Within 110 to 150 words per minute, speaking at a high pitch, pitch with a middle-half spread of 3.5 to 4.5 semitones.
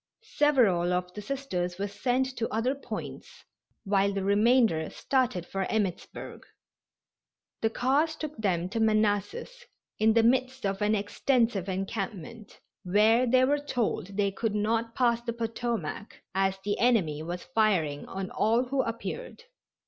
Yes: average, 140 wpm; high, 220 Hz; average, 4.2 semitones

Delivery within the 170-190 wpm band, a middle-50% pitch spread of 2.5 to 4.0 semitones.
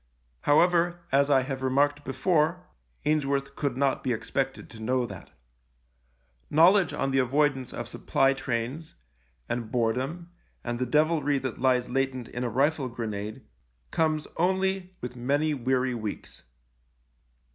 No: average, 140 wpm; average, 3.5 semitones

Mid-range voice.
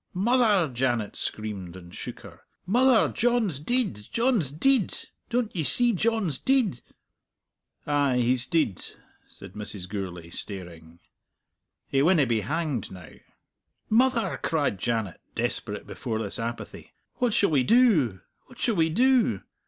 Yes: medium, 145 Hz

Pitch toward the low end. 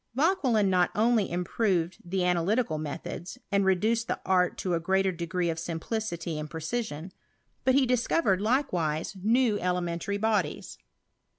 No: high, 190 Hz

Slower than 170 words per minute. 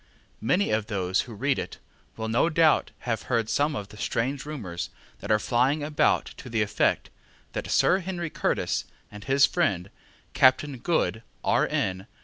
Yes: average, 160 wpm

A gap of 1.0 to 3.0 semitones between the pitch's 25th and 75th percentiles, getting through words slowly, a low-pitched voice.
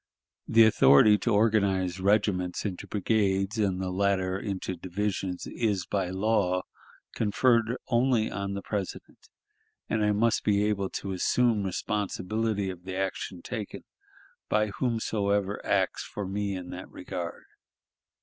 Yes: narrow, 2.4 semitones; slow, 130 wpm; low, 100 Hz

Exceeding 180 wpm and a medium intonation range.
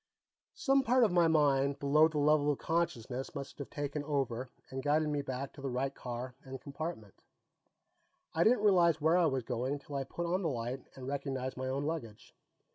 Yes: average, 200 wpm; average, 3.4 semitones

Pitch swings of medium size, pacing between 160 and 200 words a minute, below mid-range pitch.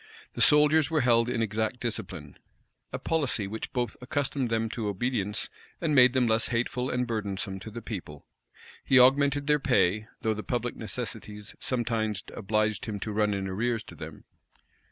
Yes: average, 3.1 semitones; average, 170 wpm; low, 115 Hz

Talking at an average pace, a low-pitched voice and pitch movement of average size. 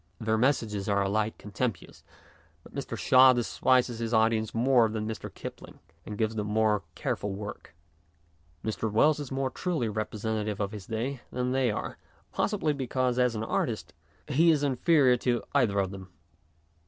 Yes: average, 160 wpm; low, 115 Hz; average, 3.3 semitones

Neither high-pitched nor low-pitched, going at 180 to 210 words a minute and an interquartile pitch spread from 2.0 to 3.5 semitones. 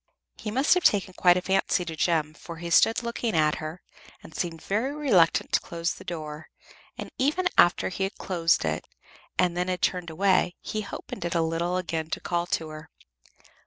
Yes: medium, 175 Hz; average, 200 wpm; average, 2.9 semitones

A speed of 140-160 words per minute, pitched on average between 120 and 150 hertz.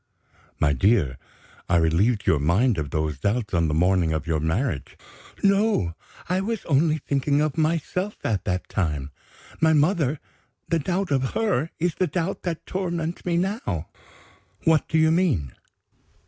Yes: average, 155 wpm; low, 135 Hz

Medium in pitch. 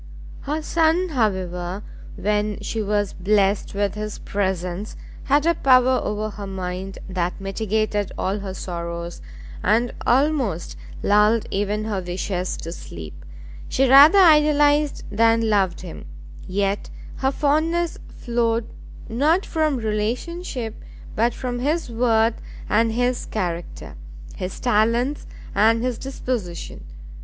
No: high, 215 Hz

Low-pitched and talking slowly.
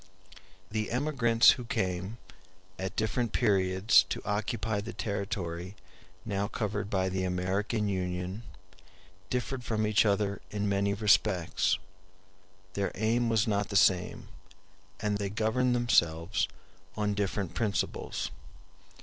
Yes: low, 105 Hz; slow, 115 wpm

